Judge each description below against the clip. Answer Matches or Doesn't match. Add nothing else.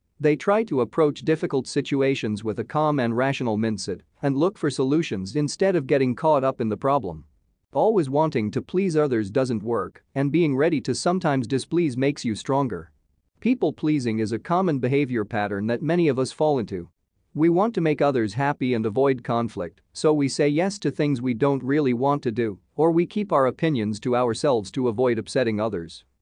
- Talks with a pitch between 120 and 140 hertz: Matches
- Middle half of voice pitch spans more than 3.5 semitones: Matches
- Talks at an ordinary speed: Matches